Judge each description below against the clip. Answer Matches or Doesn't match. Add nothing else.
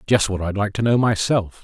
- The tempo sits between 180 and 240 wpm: Doesn't match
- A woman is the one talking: Doesn't match